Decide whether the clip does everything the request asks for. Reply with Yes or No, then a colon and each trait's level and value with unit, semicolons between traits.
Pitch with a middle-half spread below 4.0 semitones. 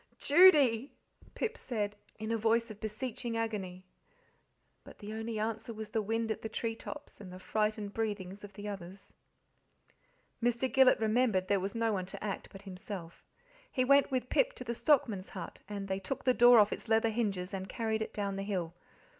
Yes: average, 2.8 semitones